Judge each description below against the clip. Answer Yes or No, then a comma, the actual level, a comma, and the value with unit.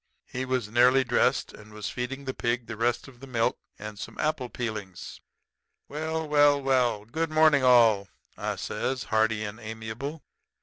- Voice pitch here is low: Yes, low, 125 Hz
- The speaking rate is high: No, average, 165 wpm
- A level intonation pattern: No, average, 3.7 semitones